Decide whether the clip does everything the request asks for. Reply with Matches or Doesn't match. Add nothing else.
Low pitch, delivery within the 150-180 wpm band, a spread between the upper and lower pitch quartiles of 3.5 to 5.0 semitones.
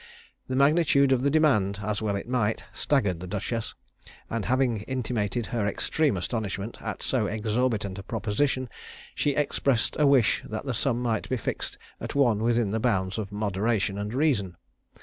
Matches